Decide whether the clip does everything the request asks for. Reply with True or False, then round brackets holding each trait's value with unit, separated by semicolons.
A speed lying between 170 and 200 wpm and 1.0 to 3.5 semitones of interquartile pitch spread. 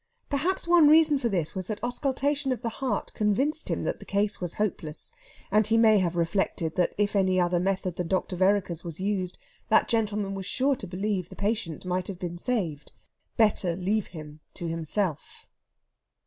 False (185 wpm; 4.3 semitones)